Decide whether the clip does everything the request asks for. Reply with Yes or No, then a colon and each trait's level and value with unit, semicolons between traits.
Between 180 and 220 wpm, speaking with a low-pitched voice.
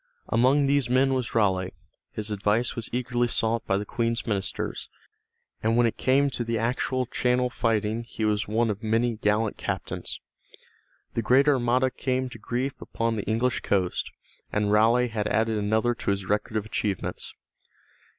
No: average, 165 wpm; low, 115 Hz